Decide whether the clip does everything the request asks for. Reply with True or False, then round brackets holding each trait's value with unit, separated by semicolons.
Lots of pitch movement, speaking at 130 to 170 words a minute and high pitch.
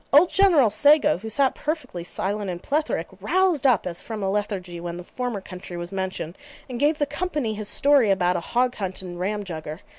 False (7.7 semitones; 200 wpm; 210 Hz)